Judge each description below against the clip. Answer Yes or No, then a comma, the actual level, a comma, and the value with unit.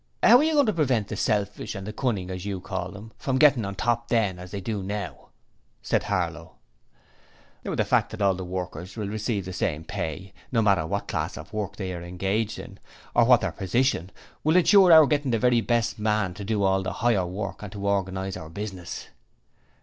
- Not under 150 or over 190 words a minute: No, fast, 205 wpm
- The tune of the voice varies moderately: Yes, average, 3.6 semitones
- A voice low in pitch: Yes, low, 100 Hz